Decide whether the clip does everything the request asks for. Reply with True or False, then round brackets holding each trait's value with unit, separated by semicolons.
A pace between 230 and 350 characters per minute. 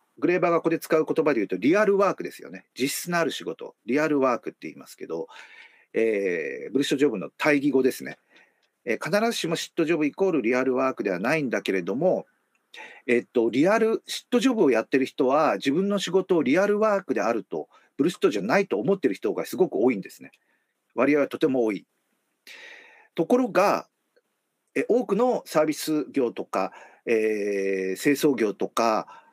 False (400 characters per minute)